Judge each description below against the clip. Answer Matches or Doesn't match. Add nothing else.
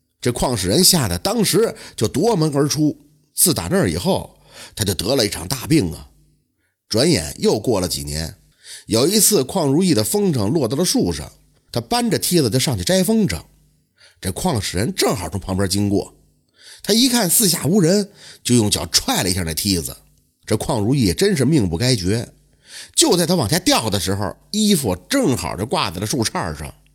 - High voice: Doesn't match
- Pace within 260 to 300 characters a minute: Matches